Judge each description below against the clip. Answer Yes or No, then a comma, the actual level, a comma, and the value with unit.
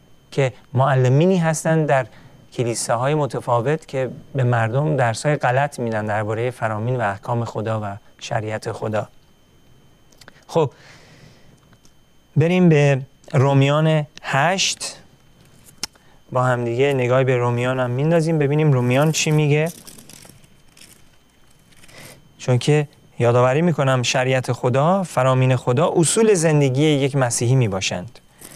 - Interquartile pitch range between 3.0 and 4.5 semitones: Yes, average, 3.4 semitones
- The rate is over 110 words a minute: No, slow, 105 wpm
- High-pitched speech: No, low, 135 Hz